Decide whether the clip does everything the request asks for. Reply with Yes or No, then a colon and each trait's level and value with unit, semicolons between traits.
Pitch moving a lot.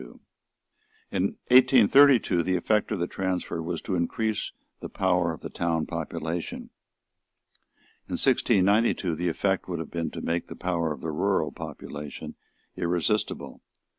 No: average, 3.2 semitones